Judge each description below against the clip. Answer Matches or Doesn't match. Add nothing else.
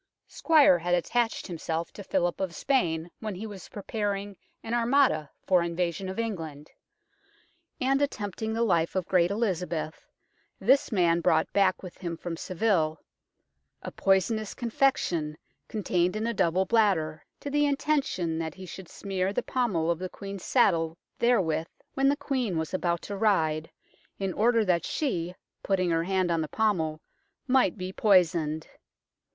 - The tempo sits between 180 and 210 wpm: Doesn't match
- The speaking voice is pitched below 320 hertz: Matches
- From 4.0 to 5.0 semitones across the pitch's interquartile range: Matches